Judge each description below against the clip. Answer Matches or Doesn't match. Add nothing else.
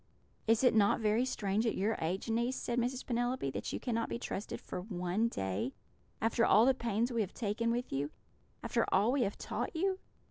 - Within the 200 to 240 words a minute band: Matches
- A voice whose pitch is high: Matches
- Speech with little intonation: Doesn't match